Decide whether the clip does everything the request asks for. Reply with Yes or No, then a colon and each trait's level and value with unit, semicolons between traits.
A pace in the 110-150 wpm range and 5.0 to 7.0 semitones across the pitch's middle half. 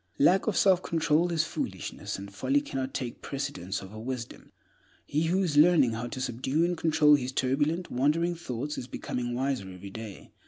No: average, 180 wpm; wide, 5.4 semitones